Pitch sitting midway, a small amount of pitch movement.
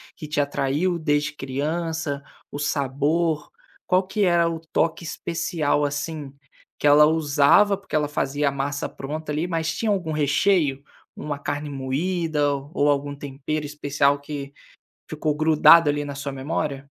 Yes: medium, 150 Hz; narrow, 2.3 semitones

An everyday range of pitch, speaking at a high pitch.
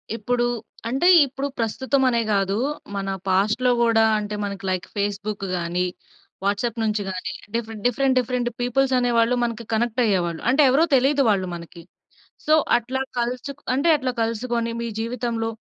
Yes: average, 3.7 semitones; high, 230 Hz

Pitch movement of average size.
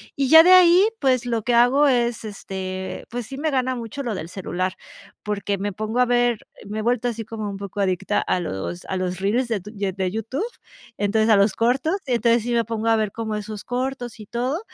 Yes: average, 3.6 semitones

